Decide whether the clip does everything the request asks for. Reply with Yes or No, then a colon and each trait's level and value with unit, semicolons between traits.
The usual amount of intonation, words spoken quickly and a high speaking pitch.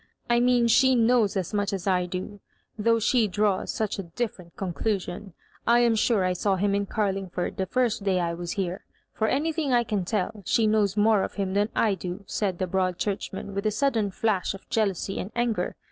Yes: average, 3.0 semitones; fast, 210 wpm; high, 205 Hz